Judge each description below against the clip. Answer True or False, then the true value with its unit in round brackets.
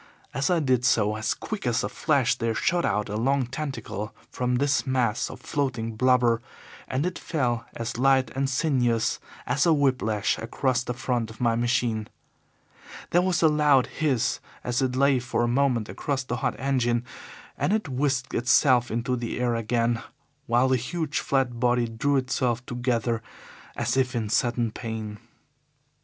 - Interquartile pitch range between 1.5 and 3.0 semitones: True (2.7 semitones)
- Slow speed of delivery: False (170 wpm)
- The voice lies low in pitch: True (125 Hz)